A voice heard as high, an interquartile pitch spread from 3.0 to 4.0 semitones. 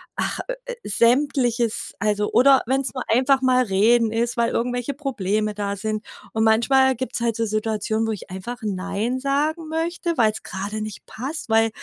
Yes: high, 230 Hz; average, 3.5 semitones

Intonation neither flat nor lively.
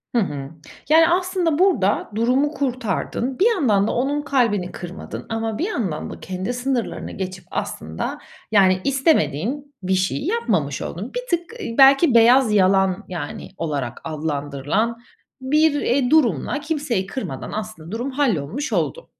No: wide, 7.3 semitones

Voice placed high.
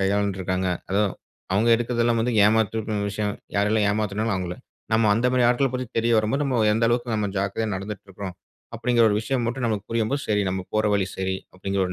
No: low, 110 Hz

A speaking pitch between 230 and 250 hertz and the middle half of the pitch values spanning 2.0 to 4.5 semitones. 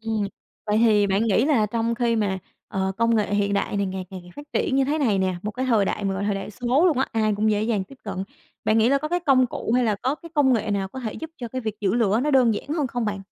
No: high, 220 Hz; average, 4.2 semitones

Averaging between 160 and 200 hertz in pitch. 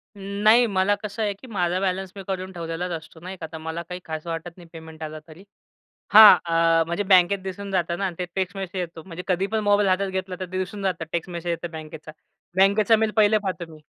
Yes: medium, 185 Hz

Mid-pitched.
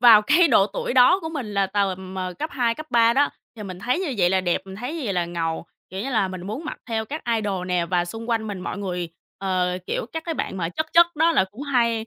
No: high, 210 Hz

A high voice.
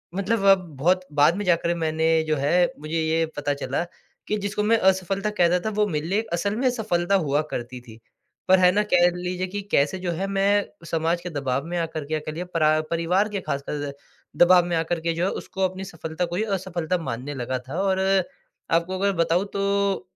No: medium, 175 Hz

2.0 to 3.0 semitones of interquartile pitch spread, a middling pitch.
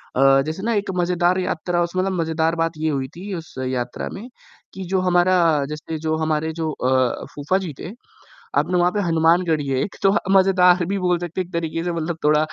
Yes: narrow, 2.6 semitones; medium, 170 Hz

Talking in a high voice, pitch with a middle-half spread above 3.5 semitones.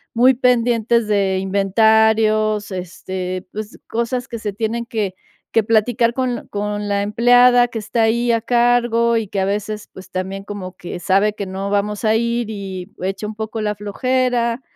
No: high, 215 Hz; average, 2.8 semitones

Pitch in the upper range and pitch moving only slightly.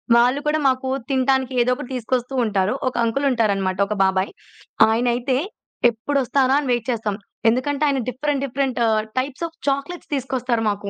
No: very high, 255 Hz; average, 3.2 semitones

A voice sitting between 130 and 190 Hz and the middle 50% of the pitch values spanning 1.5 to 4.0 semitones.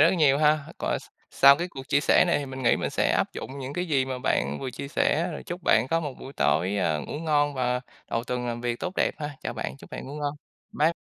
Yes: medium, 140 Hz; average, 3.6 semitones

